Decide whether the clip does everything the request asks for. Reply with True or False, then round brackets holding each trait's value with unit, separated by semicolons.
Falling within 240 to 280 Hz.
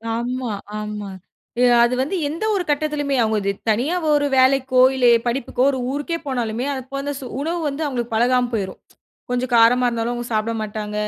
True (250 Hz)